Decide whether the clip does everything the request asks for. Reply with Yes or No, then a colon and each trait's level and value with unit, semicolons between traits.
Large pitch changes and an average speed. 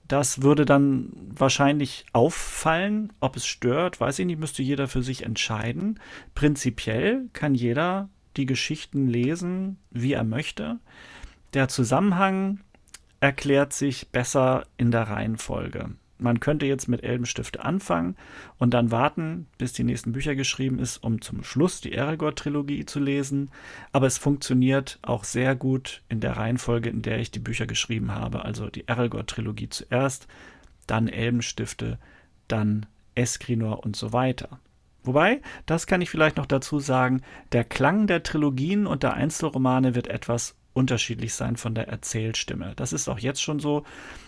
No: average, 3.6 semitones; average, 150 wpm